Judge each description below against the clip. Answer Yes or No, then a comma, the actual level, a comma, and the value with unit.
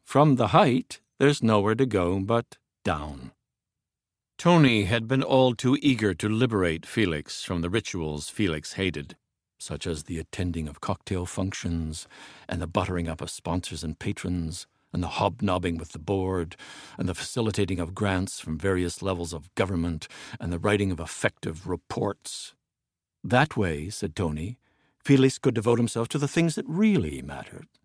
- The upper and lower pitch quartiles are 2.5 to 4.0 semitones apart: No, wide, 5.4 semitones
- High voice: No, very low, 95 Hz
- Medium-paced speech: Yes, average, 160 wpm